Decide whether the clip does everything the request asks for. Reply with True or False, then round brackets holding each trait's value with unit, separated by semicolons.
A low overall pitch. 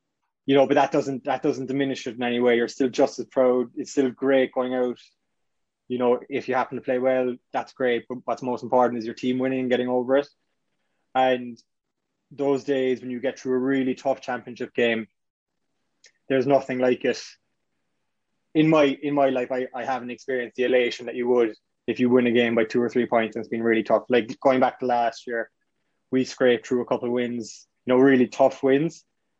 True (125 Hz)